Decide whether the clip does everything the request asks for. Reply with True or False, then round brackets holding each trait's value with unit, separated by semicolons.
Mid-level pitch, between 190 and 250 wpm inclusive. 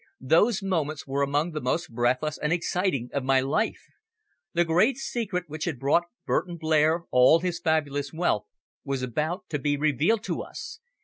False (155 Hz; 170 wpm)